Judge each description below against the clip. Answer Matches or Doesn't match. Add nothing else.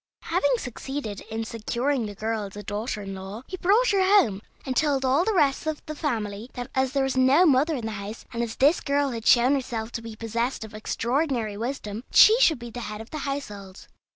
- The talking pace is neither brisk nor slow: Doesn't match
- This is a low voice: Doesn't match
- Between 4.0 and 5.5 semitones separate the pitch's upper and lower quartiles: Matches